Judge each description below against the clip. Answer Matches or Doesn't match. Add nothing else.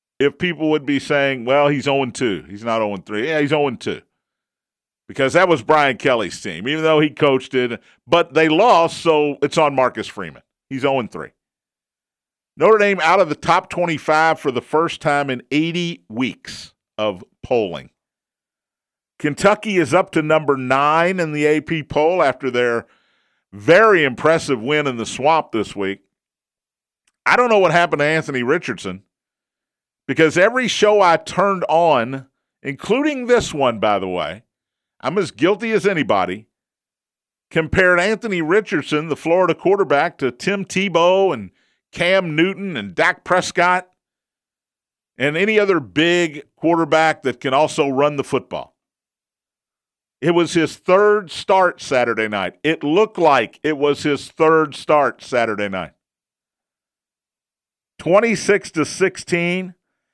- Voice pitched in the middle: Matches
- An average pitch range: Matches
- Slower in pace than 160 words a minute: Matches